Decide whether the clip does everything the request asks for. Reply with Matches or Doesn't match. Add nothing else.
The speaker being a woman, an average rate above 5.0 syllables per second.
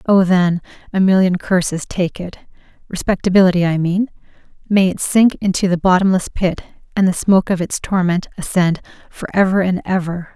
Matches